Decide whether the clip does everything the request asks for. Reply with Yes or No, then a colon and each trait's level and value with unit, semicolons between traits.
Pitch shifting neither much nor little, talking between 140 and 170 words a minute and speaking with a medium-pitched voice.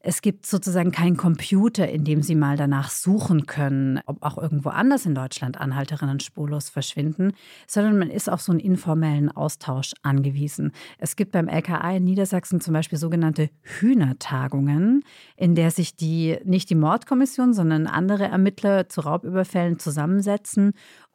Yes: average, 4.3 semitones; average, 150 wpm; medium, 170 Hz